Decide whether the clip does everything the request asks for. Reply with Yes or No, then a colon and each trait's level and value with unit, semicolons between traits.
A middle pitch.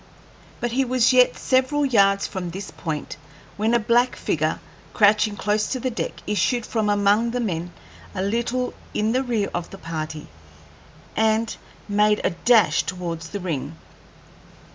No: high, 210 Hz